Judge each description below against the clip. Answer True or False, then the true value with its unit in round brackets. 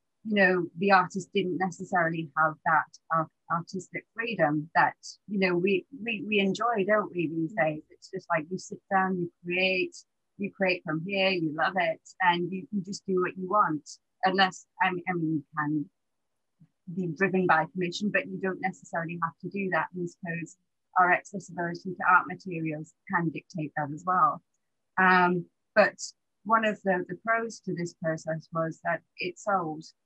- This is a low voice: False (180 Hz)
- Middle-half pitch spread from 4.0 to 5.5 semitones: False (2.7 semitones)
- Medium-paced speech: True (175 wpm)